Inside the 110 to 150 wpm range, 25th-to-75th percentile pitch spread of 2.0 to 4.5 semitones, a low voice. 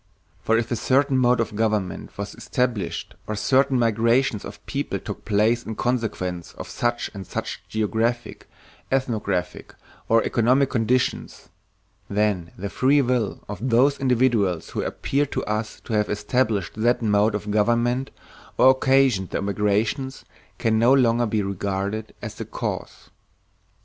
Yes: average, 145 wpm; average, 3.3 semitones; low, 115 Hz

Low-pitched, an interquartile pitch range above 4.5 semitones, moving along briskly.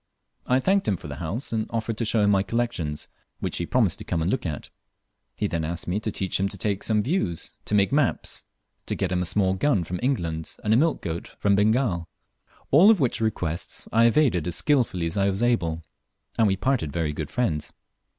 Yes: low, 100 Hz; wide, 5.6 semitones; fast, 220 wpm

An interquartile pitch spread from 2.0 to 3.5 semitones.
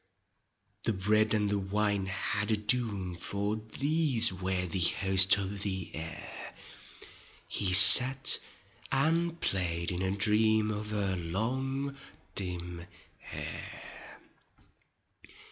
Yes: average, 2.8 semitones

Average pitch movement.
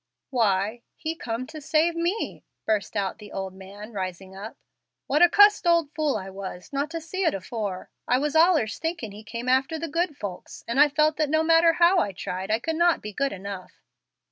No: wide, 8.2 semitones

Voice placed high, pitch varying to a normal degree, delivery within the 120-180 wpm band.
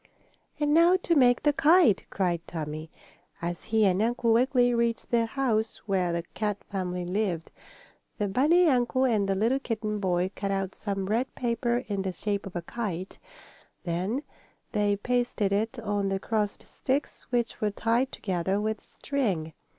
Yes: high, 215 Hz; average, 4.1 semitones; average, 165 wpm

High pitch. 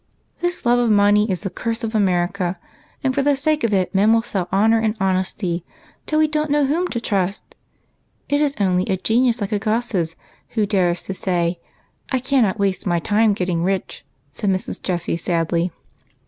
Yes: high, 205 Hz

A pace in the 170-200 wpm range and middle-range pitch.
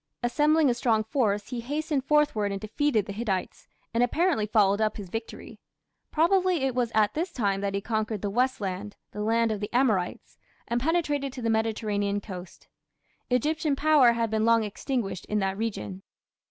No: average, 180 wpm; high, 225 Hz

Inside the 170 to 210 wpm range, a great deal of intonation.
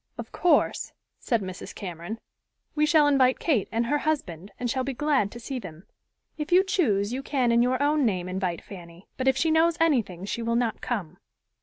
Yes: average, 200 wpm; wide, 7.0 semitones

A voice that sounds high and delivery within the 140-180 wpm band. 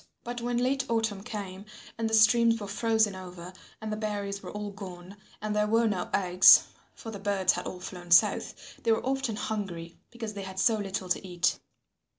No: high, 205 Hz; average, 195 wpm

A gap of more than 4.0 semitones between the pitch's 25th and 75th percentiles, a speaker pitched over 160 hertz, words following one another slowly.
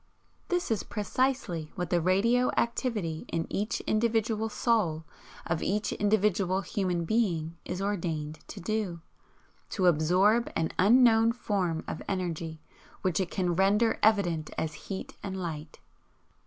Yes: average, 4.5 semitones; high, 190 Hz; slow, 130 wpm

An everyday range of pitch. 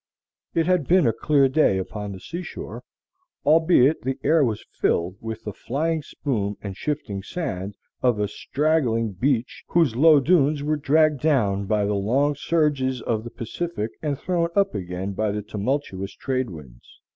No: wide, 6.7 semitones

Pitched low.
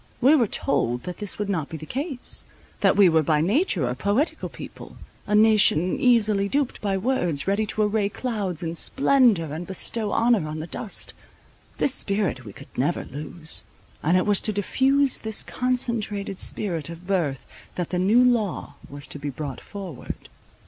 No: high, 200 Hz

